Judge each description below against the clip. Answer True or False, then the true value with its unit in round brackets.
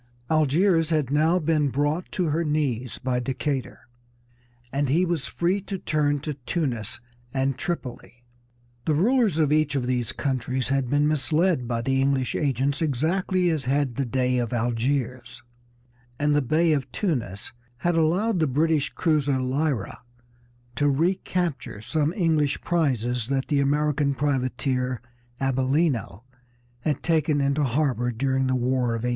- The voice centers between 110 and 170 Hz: True (140 Hz)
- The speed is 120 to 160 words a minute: True (145 wpm)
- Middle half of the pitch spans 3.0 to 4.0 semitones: True (3.6 semitones)